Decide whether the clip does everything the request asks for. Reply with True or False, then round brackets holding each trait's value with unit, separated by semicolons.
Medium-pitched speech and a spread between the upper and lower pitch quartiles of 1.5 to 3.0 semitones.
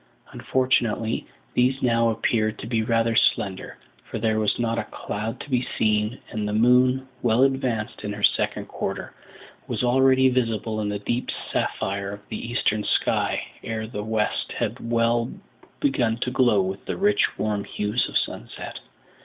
False (115 Hz; 2.7 semitones)